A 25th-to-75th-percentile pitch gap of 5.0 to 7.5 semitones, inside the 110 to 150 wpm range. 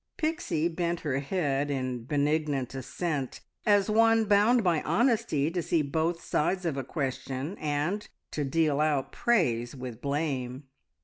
No: average, 4.6 semitones; average, 140 wpm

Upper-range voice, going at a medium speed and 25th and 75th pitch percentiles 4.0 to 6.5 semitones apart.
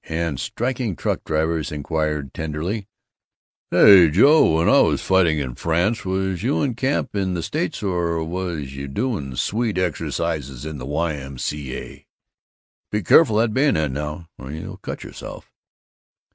No: very low, 85 Hz; average, 160 wpm; average, 4.8 semitones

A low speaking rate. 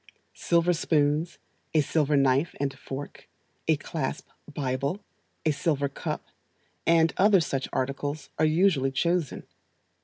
Yes: slow, 120 wpm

